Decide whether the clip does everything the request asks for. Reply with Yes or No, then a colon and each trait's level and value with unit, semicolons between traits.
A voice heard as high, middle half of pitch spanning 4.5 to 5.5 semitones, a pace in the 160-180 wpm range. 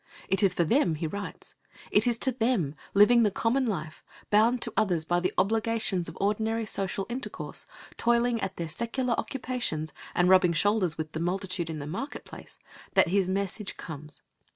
Yes: high, 200 Hz; average, 4.8 semitones; average, 175 wpm